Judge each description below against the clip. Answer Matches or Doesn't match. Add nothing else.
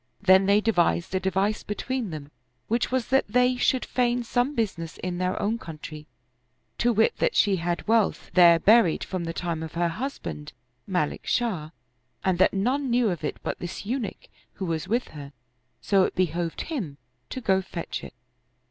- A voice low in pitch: Doesn't match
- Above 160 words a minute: Matches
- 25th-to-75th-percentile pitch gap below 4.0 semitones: Doesn't match